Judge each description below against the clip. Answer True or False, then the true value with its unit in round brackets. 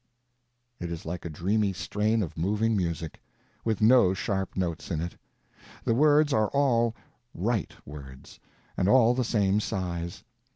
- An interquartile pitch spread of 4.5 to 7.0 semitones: True (4.8 semitones)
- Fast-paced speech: False (150 wpm)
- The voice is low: True (100 Hz)